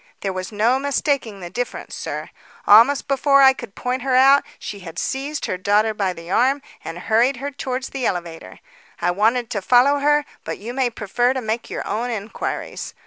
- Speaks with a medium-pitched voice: No, high, 240 Hz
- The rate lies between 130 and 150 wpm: No, average, 195 wpm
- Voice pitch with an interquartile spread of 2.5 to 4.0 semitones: No, average, 4.8 semitones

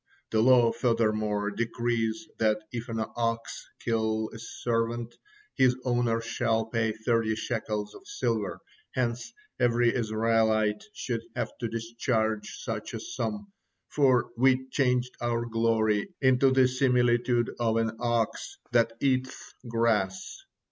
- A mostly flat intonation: Yes, narrow, 1.8 semitones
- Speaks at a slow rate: Yes, slow, 125 wpm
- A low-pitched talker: Yes, low, 115 Hz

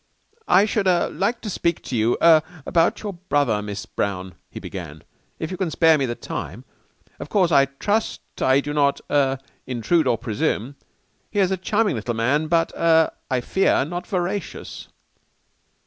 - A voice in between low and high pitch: Yes, medium, 155 Hz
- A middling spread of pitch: No, wide, 6.2 semitones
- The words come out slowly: No, average, 170 wpm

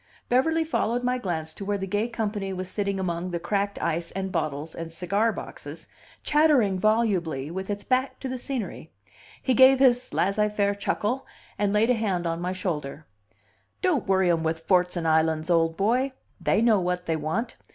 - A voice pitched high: Yes, high, 195 Hz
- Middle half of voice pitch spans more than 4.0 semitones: Yes, average, 5.2 semitones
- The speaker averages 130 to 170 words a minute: No, average, 185 wpm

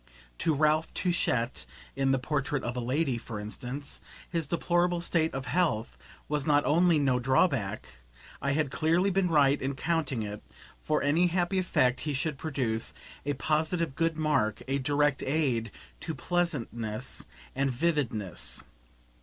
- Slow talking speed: No, average, 145 wpm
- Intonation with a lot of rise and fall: No, average, 4.4 semitones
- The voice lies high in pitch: No, medium, 145 Hz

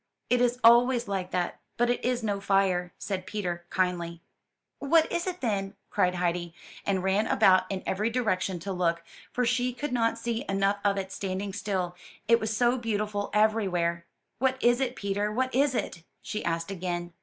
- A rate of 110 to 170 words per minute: No, average, 180 wpm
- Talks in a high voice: Yes, high, 200 Hz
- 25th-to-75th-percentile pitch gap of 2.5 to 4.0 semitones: No, average, 4.6 semitones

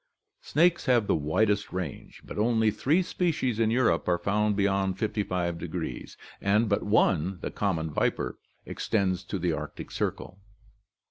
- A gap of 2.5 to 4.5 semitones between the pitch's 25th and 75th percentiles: Yes, average, 3.4 semitones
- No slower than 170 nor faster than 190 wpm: No, average, 140 wpm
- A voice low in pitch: Yes, low, 100 Hz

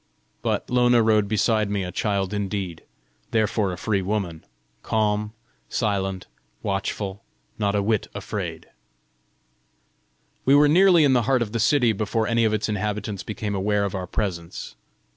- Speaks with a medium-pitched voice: No, low, 105 Hz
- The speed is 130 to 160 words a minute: Yes, average, 150 wpm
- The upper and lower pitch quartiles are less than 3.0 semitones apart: Yes, narrow, 2.4 semitones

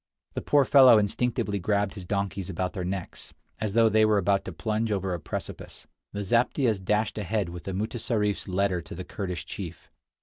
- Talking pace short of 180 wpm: No, average, 190 wpm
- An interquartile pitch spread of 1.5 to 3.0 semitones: Yes, average, 2.7 semitones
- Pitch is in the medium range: No, low, 100 Hz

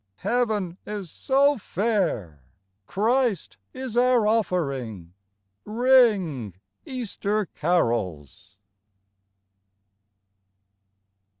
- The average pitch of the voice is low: No, high, 205 Hz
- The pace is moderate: No, slow, 60 wpm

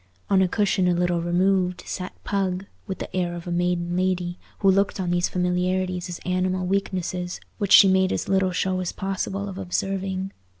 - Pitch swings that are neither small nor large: No, narrow, 1.3 semitones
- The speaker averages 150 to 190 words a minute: Yes, average, 185 wpm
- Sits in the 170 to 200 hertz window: Yes, medium, 185 Hz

